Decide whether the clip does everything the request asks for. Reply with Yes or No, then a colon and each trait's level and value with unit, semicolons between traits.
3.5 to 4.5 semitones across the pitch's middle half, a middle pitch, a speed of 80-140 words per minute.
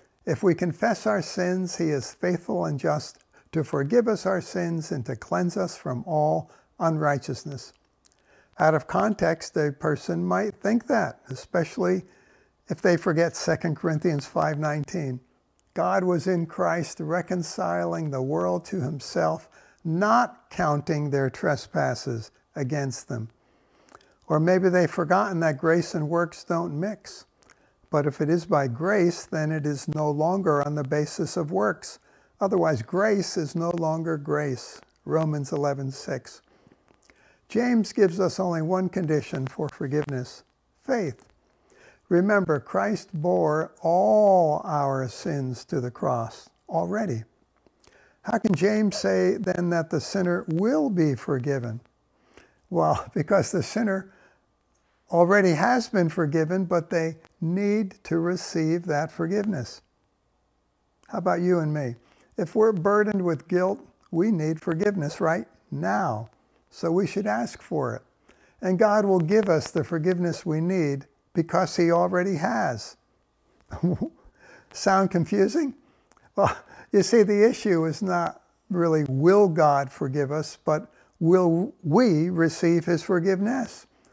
Yes: average, 4.0 semitones; medium, 170 Hz; slow, 135 wpm